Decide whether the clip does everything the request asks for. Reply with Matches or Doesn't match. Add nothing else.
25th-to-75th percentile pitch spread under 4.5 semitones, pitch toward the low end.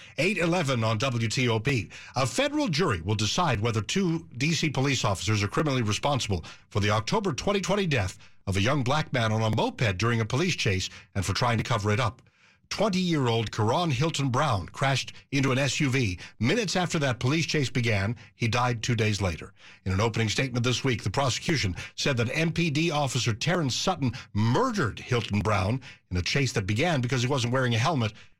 Doesn't match